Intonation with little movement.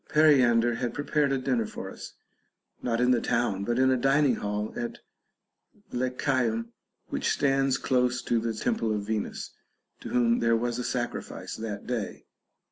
Yes: narrow, 2.2 semitones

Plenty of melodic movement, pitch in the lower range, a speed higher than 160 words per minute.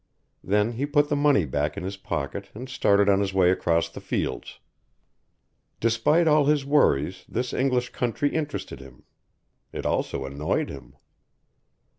No: wide, 8.1 semitones; low, 105 Hz; average, 150 wpm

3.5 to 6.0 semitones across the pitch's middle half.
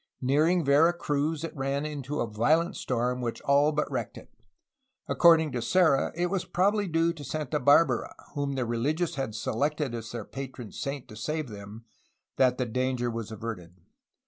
Yes: average, 4.7 semitones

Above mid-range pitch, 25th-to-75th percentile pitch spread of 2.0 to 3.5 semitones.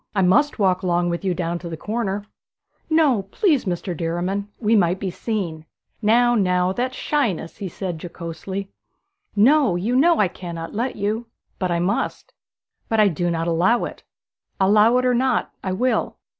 No: high, 195 Hz; average, 5.0 semitones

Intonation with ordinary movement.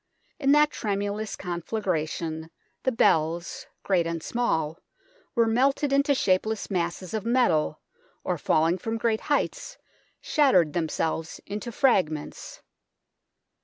No: wide, 6.3 semitones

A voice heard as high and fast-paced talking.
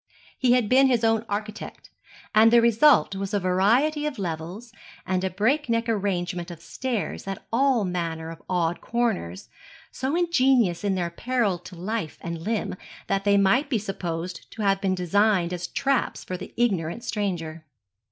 No: high, 200 Hz; average, 165 wpm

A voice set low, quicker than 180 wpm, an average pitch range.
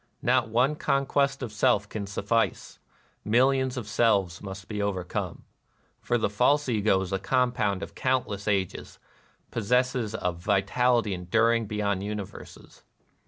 No: low, 110 Hz; slow, 135 wpm; average, 3.9 semitones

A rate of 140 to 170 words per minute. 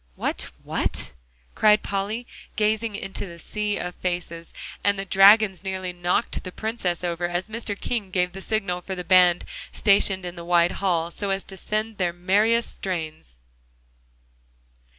Yes: average, 150 wpm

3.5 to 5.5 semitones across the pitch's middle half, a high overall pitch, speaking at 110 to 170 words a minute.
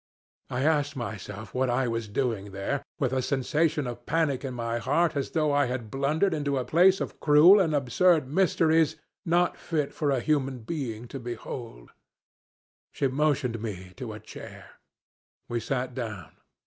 No: average, 4.4 semitones; low, 135 Hz; average, 165 wpm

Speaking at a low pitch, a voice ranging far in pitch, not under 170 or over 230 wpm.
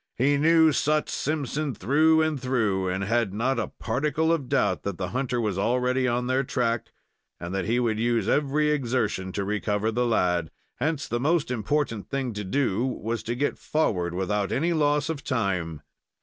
Yes: low, 125 Hz; wide, 5.7 semitones; average, 180 wpm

